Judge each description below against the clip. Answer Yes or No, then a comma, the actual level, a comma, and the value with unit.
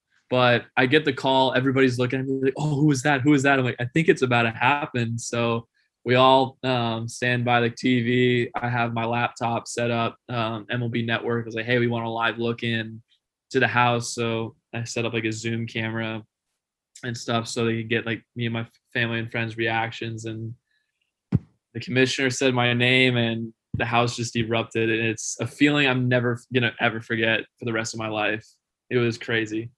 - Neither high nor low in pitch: No, low, 120 Hz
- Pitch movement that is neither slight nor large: No, narrow, 1.6 semitones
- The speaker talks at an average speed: No, fast, 210 wpm